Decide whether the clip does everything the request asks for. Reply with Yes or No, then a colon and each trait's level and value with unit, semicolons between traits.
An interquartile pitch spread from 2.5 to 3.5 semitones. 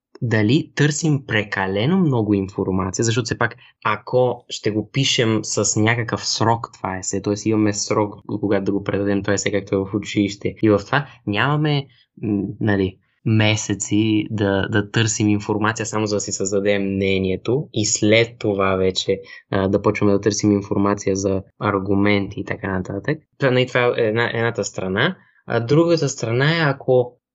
Yes: average, 3.2 semitones